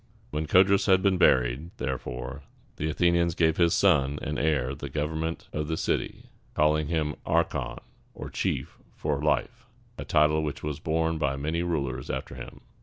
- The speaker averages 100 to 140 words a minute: No, average, 165 wpm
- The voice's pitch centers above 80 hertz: No, very low, 75 Hz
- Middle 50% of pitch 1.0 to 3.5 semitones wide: Yes, narrow, 2.6 semitones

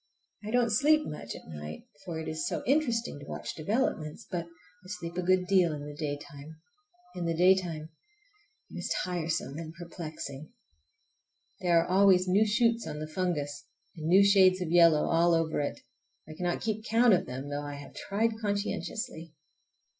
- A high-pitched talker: No, medium, 170 Hz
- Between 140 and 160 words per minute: No, average, 175 wpm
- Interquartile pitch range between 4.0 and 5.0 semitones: Yes, average, 4.3 semitones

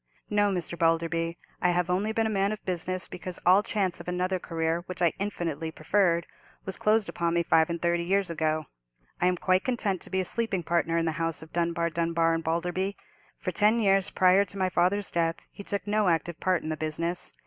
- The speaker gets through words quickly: Yes, fast, 215 wpm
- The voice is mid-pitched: Yes, medium, 175 Hz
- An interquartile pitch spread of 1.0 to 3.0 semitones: Yes, narrow, 2.6 semitones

